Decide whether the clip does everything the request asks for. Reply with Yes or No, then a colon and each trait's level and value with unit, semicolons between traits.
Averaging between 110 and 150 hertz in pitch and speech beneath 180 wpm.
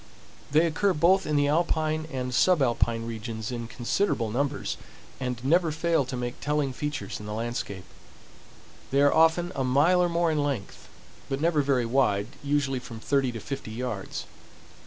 Yes: medium, 140 Hz; average, 160 wpm